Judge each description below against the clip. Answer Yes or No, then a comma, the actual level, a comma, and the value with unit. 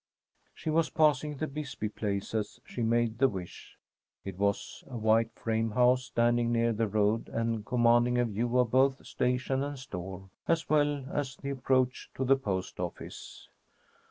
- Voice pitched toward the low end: Yes, low, 120 Hz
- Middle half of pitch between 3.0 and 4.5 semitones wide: Yes, average, 3.3 semitones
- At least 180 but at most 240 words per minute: No, average, 165 wpm